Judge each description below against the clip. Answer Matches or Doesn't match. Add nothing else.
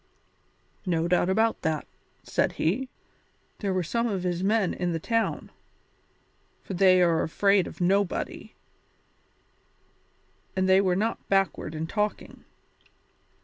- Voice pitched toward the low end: Doesn't match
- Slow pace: Matches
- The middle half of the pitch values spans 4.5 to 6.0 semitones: Doesn't match